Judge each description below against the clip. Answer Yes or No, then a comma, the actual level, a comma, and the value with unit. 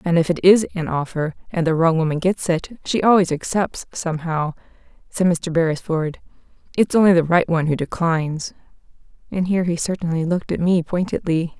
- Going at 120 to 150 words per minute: No, average, 175 wpm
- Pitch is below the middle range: No, medium, 170 Hz